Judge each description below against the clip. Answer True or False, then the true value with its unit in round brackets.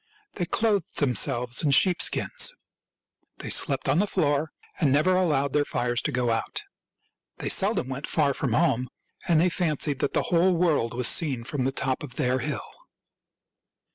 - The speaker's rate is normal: True (170 wpm)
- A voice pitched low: False (145 Hz)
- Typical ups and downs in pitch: True (4.8 semitones)